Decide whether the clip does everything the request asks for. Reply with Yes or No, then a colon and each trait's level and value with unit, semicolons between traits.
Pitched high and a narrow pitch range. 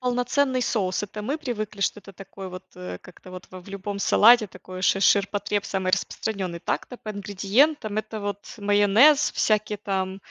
Yes: high, 205 Hz; narrow, 2.3 semitones